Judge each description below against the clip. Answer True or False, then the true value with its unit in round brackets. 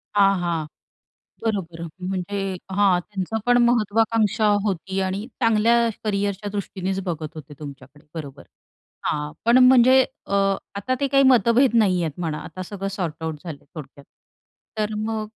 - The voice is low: False (195 Hz)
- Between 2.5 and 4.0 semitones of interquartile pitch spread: False (4.6 semitones)